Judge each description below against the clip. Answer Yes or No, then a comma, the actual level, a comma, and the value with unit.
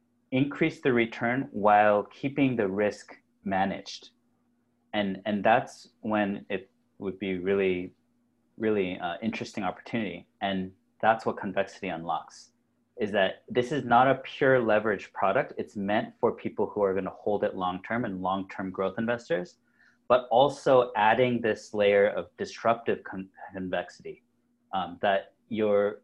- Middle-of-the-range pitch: No, low, 110 Hz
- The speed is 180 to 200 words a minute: No, average, 145 wpm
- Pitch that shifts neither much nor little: Yes, average, 3.5 semitones